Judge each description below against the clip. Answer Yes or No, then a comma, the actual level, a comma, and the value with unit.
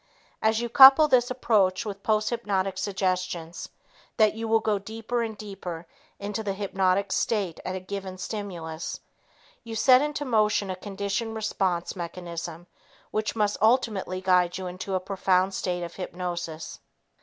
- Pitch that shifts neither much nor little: Yes, average, 3.1 semitones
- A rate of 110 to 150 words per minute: Yes, average, 145 wpm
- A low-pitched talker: No, high, 195 Hz